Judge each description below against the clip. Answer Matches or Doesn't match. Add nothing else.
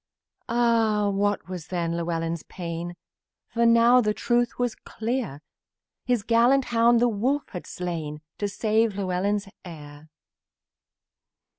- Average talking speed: Doesn't match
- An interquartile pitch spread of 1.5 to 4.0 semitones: Doesn't match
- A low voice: Doesn't match